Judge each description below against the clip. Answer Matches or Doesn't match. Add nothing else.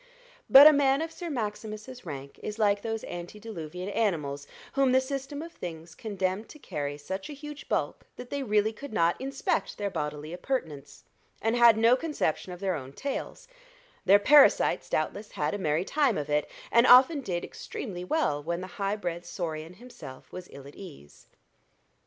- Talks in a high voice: Matches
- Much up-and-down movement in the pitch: Matches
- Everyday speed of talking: Matches